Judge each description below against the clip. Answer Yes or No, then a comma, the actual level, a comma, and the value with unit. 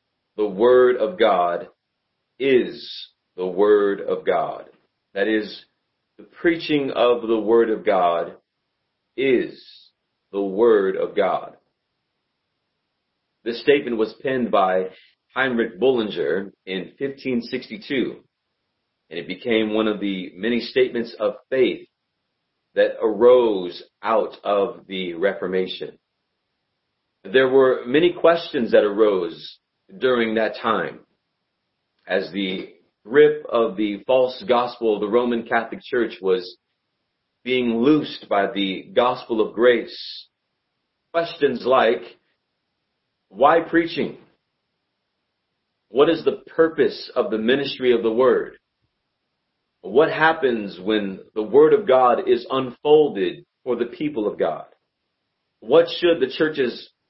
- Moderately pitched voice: No, low, 125 Hz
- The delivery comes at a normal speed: No, slow, 115 wpm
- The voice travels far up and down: Yes, wide, 7.8 semitones